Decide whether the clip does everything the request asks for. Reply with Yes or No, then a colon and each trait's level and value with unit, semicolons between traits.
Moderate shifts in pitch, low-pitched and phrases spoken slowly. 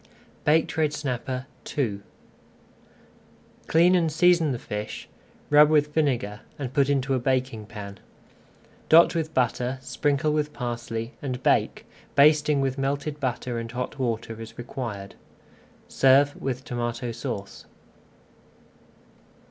Yes: average, 3.8 semitones; low, 130 Hz; slow, 120 wpm